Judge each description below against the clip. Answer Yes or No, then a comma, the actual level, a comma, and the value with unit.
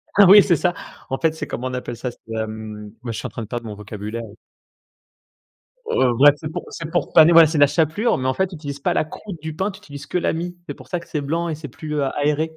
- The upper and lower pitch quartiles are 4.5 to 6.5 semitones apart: Yes, wide, 5.4 semitones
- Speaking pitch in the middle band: Yes, medium, 150 Hz